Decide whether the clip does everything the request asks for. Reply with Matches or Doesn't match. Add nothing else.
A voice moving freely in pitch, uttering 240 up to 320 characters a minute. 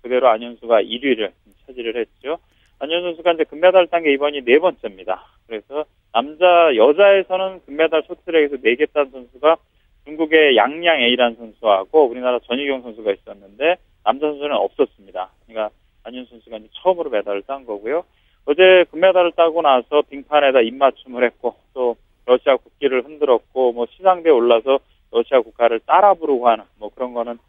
Doesn't match